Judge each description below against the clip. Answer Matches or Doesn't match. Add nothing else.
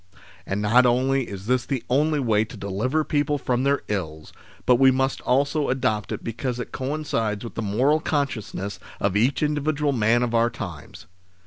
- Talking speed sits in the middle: Matches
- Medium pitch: Doesn't match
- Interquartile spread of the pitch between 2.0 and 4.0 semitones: Doesn't match